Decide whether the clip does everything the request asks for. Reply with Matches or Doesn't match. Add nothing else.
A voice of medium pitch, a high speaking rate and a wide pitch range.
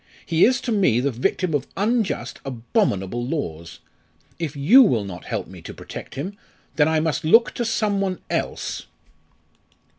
Doesn't match